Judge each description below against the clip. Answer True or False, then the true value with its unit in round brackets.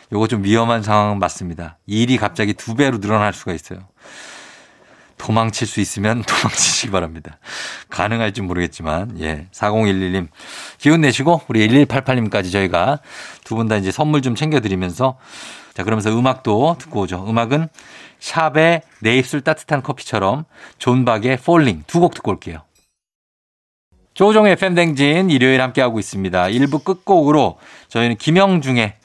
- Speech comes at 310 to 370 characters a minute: True (315 characters per minute)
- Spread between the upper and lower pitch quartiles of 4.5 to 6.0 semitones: False (6.4 semitones)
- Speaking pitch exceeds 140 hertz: False (115 Hz)